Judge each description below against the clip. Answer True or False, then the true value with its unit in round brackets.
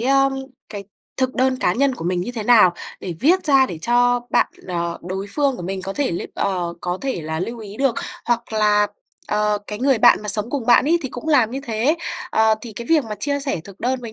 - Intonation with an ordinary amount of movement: True (5.0 semitones)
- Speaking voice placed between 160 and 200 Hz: False (230 Hz)